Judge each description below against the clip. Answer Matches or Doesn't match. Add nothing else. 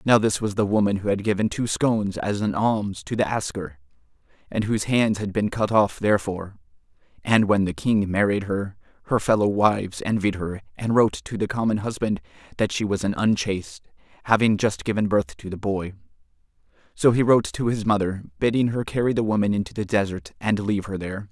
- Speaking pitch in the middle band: Doesn't match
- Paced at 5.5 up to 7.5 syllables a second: Matches